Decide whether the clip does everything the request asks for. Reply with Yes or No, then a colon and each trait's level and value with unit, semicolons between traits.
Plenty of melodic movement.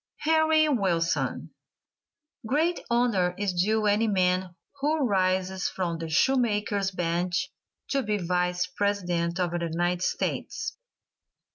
No: average, 4.6 semitones